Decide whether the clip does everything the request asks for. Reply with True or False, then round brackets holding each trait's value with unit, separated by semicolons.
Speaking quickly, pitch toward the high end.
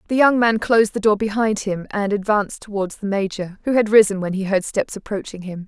True (235 wpm; 205 Hz)